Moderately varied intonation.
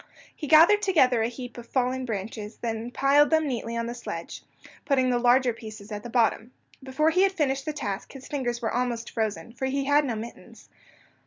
Yes: average, 3.3 semitones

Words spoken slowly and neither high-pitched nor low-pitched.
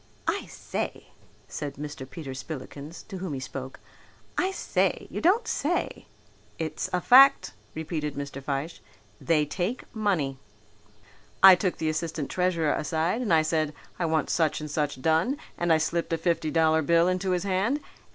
No: average, 160 wpm; medium, 160 Hz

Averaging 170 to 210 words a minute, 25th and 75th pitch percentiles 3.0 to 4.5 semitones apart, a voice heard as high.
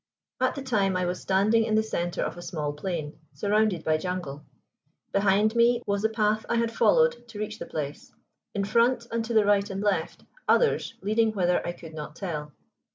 Yes: average, 200 wpm; average, 4.2 semitones; high, 205 Hz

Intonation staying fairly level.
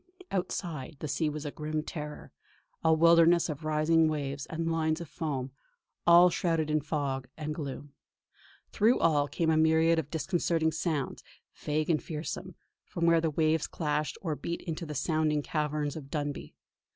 Yes: narrow, 1.8 semitones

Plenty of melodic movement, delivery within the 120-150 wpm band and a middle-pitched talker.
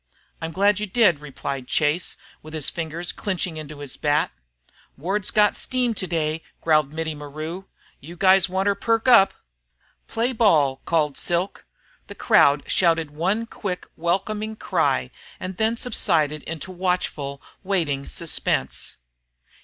No: average, 4.5 semitones; slow, 135 wpm; medium, 170 Hz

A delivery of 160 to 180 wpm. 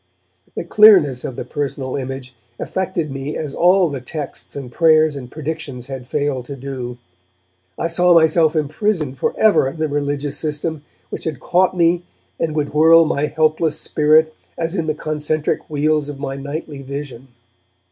Yes: average, 165 wpm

